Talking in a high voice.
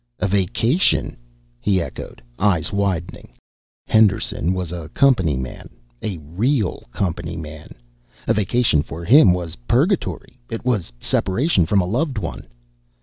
No: very low, 95 Hz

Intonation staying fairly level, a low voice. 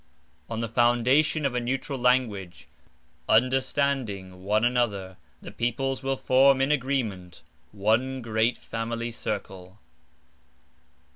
No: average, 3.8 semitones; low, 120 Hz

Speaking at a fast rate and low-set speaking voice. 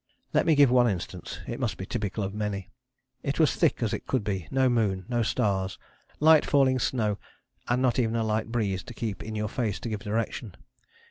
Yes: fast, 210 wpm; low, 110 Hz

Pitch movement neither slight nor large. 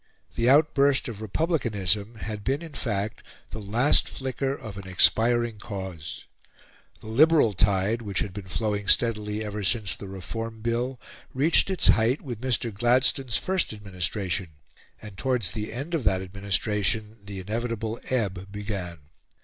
Yes: average, 3.5 semitones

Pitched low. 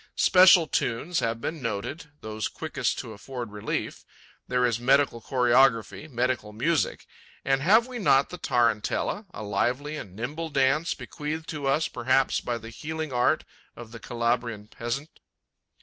Yes: low, 130 Hz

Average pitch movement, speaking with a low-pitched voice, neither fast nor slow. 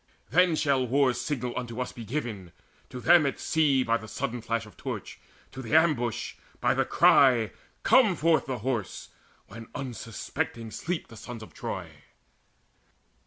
Yes: average, 4.1 semitones; low, 125 Hz; average, 155 wpm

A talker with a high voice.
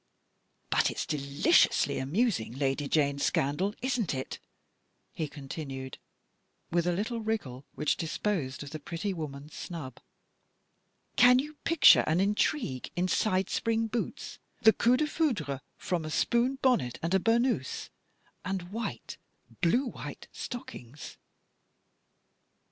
No: medium, 175 Hz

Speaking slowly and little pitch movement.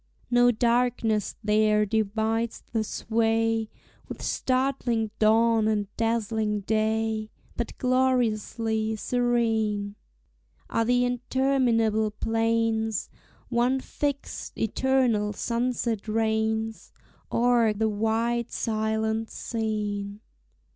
Yes: slow, 85 wpm; narrow, 1.6 semitones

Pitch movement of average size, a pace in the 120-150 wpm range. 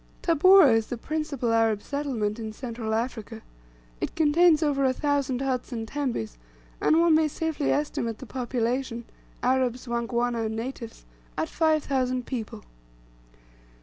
Yes: average, 4.1 semitones; average, 140 wpm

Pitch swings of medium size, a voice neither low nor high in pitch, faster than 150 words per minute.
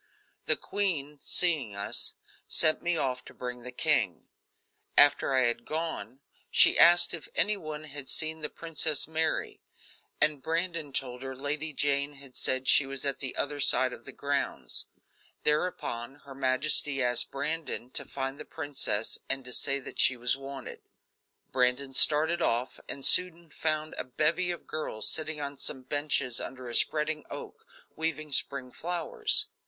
Yes: average, 3.3 semitones; medium, 145 Hz; average, 160 wpm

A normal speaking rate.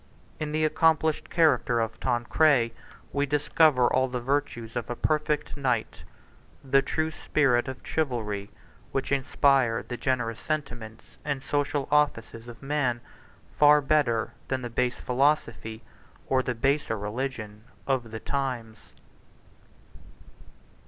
No: slow, 125 wpm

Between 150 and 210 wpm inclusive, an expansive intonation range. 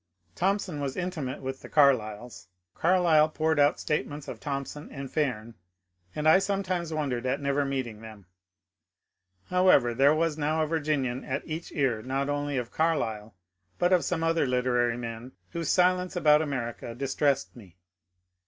No: average, 155 wpm; average, 4.1 semitones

